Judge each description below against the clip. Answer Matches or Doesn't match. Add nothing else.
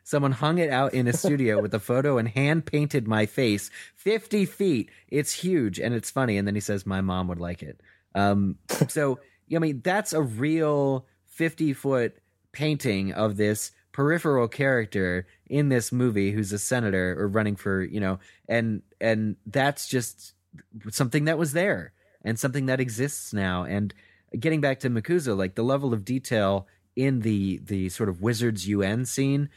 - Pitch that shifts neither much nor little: Doesn't match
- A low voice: Matches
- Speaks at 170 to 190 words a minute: Matches